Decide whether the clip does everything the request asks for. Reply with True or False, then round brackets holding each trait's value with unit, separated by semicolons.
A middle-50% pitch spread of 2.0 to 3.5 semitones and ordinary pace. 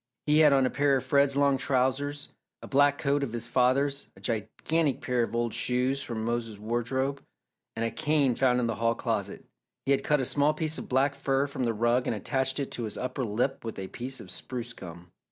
False (3.1 semitones; 225 wpm)